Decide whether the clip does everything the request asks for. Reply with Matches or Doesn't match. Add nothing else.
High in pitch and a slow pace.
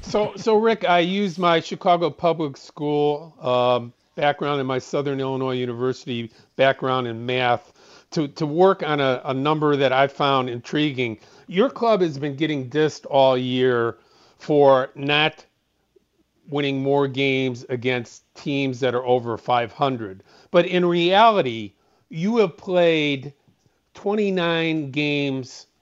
Doesn't match